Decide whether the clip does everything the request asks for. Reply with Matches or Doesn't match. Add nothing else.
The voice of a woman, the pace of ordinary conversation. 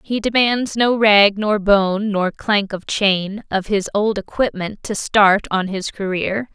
Matches